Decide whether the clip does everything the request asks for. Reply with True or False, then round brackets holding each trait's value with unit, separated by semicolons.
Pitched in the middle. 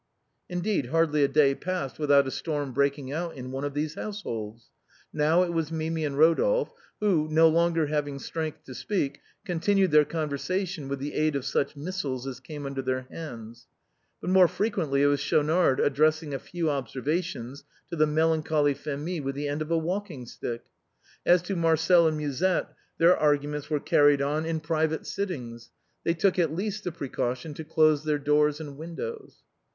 True (155 Hz)